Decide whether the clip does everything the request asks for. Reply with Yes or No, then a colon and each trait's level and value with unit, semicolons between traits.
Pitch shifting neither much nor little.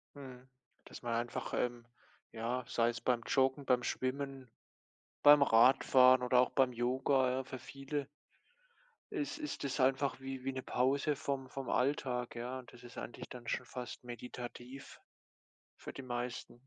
No: narrow, 1.7 semitones